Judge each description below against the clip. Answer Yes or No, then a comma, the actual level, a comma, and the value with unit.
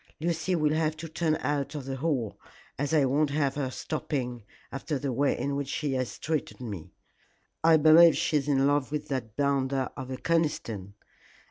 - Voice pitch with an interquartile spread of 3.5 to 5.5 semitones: No, average, 2.7 semitones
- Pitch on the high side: No, medium, 145 Hz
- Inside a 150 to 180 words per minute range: No, average, 190 wpm